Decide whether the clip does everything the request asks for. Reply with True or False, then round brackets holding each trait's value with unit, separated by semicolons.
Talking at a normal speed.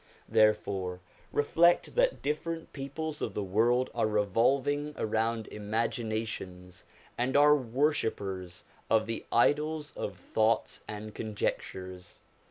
False (105 wpm)